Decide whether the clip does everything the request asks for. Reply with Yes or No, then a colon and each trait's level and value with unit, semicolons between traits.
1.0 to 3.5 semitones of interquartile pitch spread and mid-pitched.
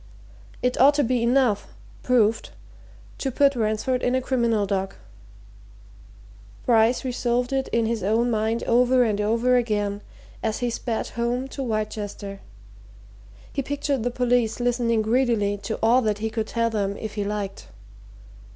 No: average, 2.7 semitones; high, 230 Hz